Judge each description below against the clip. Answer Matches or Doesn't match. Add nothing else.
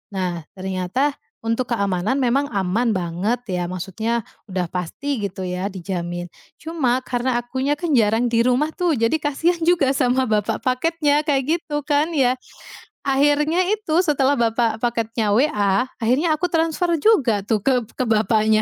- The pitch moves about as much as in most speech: Doesn't match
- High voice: Matches